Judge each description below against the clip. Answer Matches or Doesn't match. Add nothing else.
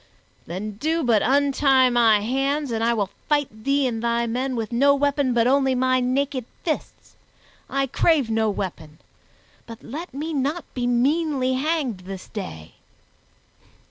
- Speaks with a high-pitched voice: Matches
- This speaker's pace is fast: Doesn't match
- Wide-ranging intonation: Doesn't match